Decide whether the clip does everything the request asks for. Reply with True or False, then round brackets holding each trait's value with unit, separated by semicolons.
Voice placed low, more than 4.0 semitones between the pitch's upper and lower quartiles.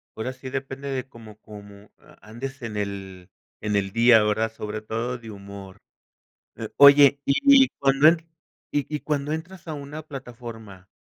True (120 Hz; 5.0 semitones)